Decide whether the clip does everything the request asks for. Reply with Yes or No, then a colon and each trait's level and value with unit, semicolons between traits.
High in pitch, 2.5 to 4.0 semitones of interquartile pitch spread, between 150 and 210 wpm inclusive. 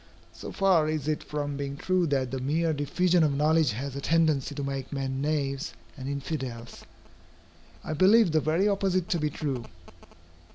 No: medium, 150 Hz; average, 3.1 semitones; average, 170 wpm